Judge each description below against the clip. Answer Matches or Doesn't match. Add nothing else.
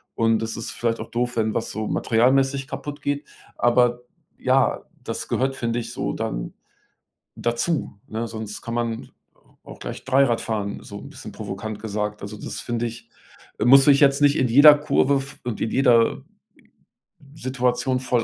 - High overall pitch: Doesn't match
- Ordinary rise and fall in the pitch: Matches